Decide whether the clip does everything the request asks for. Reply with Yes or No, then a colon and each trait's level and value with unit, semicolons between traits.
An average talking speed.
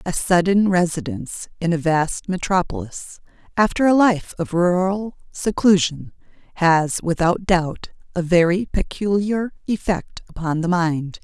No: slow, 125 wpm